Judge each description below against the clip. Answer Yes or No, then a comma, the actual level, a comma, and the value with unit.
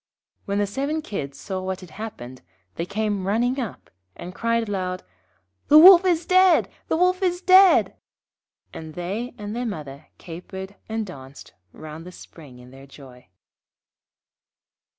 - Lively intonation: Yes, wide, 7.7 semitones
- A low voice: No, high, 200 Hz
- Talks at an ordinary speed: Yes, average, 150 wpm